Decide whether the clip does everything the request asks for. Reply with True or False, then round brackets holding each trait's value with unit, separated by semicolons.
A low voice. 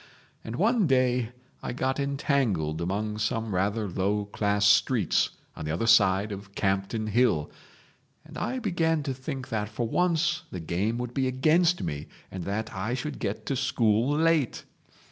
True (115 Hz)